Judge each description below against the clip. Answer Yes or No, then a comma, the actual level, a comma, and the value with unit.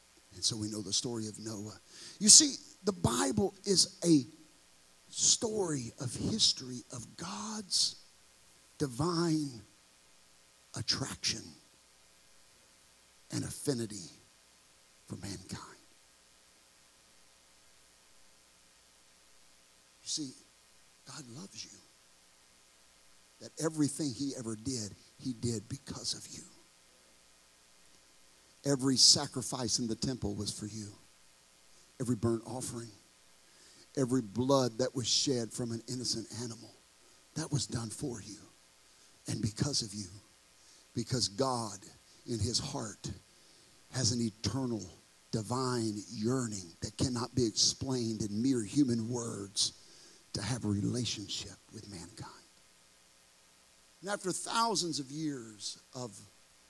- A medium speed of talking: No, slow, 105 wpm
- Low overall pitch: Yes, low, 105 Hz